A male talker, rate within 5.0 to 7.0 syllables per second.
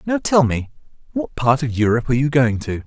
Yes: male; 6.0 syllables/s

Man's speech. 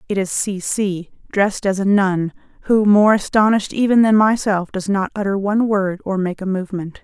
No: female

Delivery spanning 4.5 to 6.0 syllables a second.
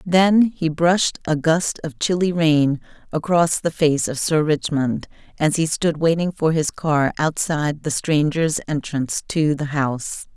No: 4.2 syllables/s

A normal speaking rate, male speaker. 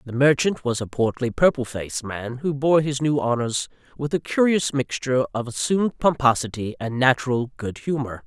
Yes: average, 175 wpm; male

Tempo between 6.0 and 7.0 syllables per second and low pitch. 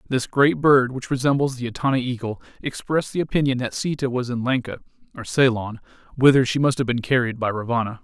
Yes: 6.1 syllables/s; low, 125 Hz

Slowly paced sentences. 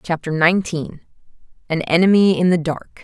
Yes: slow, 120 wpm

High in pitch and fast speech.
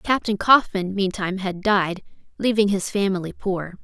No: high, 195 Hz; average, 140 wpm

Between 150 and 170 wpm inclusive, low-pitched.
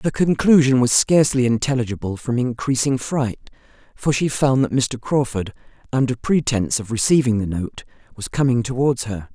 Yes: average, 155 wpm; low, 125 Hz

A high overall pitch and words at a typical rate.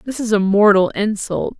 Yes: high, 205 Hz; average, 190 wpm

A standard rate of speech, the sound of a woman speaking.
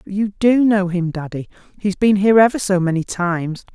No: fast, 210 wpm; female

